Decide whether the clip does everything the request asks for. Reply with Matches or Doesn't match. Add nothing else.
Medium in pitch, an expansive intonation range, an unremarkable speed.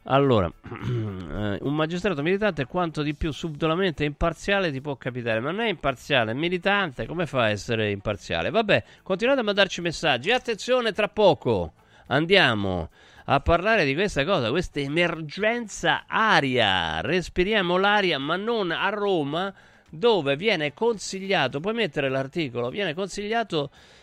Matches